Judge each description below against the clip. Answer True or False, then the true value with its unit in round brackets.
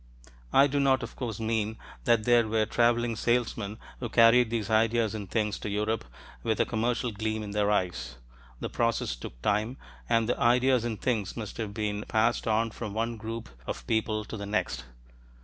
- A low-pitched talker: True (110 Hz)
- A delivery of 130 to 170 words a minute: False (185 wpm)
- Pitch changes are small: True (1.9 semitones)